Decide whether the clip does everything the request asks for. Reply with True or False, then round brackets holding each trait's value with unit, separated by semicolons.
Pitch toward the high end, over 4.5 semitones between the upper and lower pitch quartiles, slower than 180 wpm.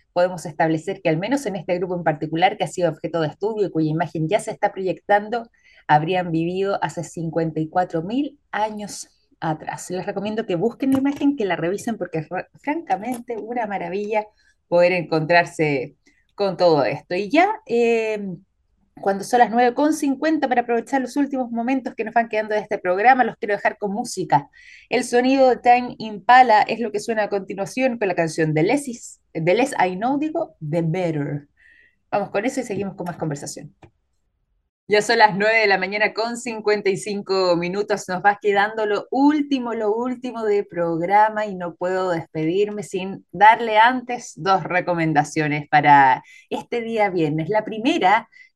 True (205 Hz; 5.2 semitones; 170 wpm)